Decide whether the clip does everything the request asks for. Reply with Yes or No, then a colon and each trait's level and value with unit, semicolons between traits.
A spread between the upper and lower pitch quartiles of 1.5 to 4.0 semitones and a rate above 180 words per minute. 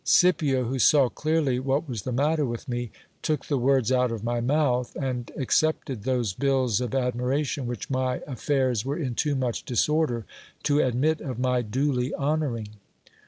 No: average, 2.8 semitones; average, 165 wpm